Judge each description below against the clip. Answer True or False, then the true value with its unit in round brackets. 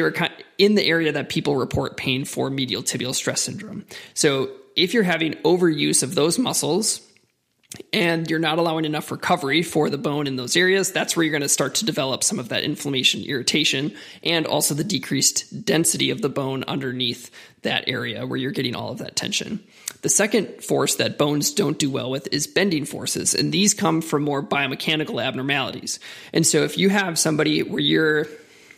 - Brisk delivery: False (190 wpm)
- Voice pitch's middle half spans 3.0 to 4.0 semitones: True (3.4 semitones)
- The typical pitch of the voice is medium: True (155 Hz)